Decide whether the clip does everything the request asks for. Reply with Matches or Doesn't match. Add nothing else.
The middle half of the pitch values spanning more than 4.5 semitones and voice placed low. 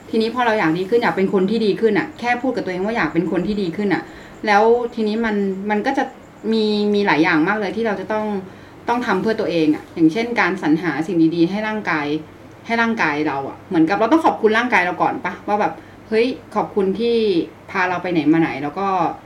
Doesn't match